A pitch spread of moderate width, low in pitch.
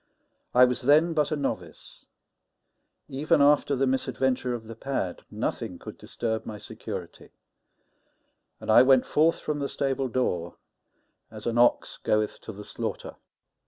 Yes: average, 3.7 semitones; low, 130 Hz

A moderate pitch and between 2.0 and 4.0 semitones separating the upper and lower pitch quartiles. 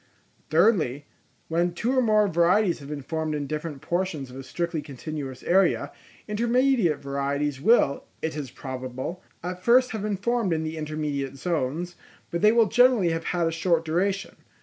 No: medium, 165 Hz; average, 5.3 semitones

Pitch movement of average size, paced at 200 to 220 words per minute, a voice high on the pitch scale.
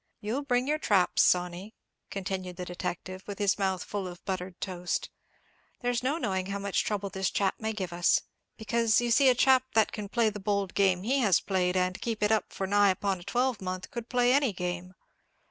Yes: average, 3.9 semitones; fast, 205 wpm; high, 200 Hz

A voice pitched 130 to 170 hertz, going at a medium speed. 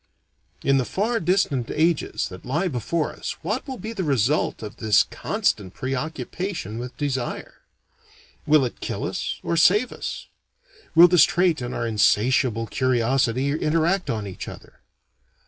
Yes: medium, 140 Hz; average, 145 wpm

